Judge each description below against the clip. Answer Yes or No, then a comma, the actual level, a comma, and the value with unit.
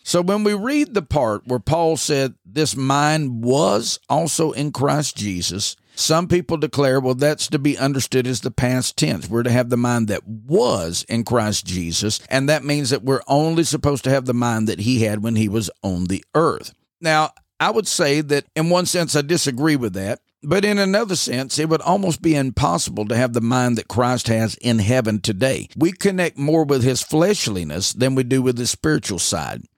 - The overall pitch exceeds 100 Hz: Yes, low, 135 Hz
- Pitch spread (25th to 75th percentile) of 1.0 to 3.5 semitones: No, average, 4.9 semitones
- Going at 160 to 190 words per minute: No, fast, 205 wpm